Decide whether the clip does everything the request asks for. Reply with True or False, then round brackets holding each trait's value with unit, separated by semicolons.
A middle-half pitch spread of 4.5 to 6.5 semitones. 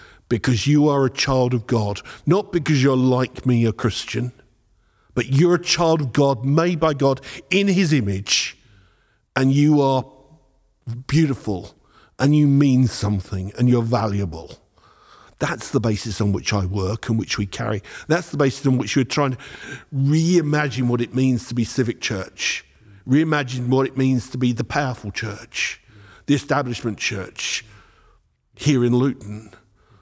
True (4.8 semitones)